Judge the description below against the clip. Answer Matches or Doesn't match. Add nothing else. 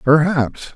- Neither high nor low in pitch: Matches